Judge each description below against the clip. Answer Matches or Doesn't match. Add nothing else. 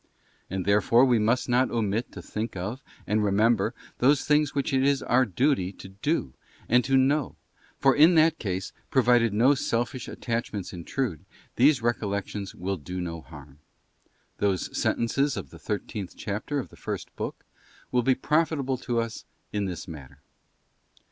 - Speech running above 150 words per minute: Matches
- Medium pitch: Doesn't match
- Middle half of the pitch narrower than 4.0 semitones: Doesn't match